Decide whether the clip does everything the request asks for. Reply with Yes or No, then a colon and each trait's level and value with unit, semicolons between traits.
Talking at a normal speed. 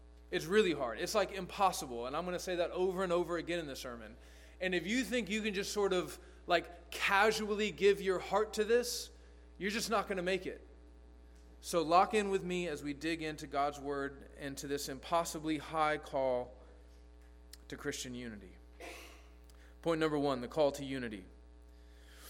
Yes: average, 185 wpm